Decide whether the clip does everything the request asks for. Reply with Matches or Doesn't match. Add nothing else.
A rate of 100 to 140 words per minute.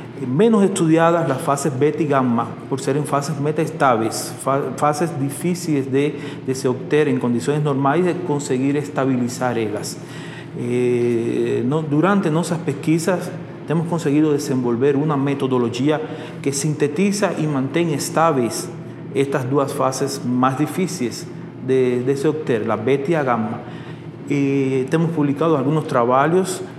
Matches